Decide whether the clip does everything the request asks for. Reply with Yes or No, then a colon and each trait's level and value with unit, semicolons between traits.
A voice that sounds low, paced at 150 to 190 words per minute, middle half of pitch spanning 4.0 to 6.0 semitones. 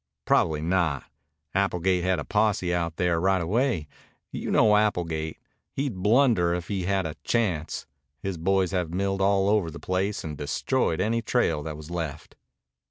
No: very low, 90 Hz; average, 165 wpm; average, 3.3 semitones